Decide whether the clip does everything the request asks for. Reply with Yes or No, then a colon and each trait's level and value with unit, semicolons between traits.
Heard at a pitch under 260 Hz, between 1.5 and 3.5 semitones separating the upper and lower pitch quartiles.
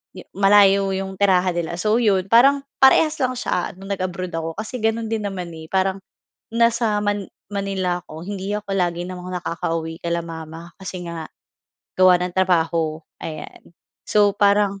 Yes: high, 190 Hz; average, 3.0 semitones